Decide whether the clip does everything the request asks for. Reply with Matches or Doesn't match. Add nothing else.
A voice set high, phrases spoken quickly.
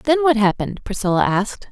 Doesn't match